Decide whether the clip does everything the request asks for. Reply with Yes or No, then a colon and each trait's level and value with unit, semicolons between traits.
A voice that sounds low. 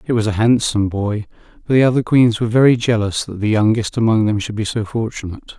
Yes: low, 110 Hz